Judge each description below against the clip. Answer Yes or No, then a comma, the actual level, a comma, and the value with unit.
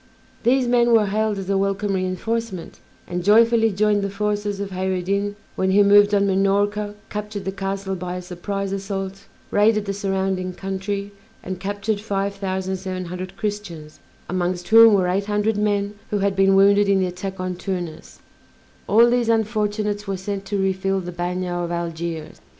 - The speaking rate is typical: Yes, average, 175 wpm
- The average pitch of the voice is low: No, high, 195 Hz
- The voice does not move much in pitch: Yes, narrow, 1.8 semitones